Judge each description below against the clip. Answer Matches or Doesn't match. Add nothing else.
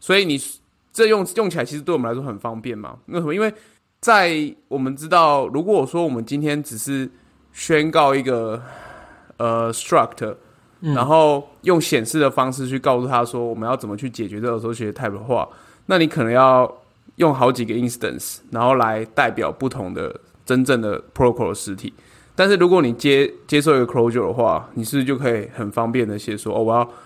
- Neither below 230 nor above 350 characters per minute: Matches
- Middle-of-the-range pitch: Doesn't match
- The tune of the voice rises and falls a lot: Doesn't match